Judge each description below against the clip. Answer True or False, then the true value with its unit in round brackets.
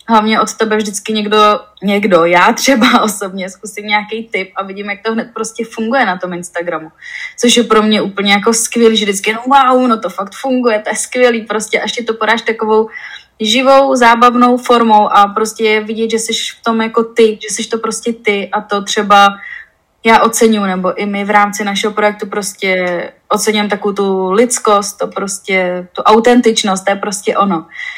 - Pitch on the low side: False (215 Hz)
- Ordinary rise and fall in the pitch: False (2.1 semitones)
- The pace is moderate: False (190 wpm)